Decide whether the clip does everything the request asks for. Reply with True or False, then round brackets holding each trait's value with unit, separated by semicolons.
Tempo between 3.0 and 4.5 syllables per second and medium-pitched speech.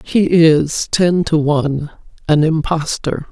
True (3.5 syllables/s; 160 Hz)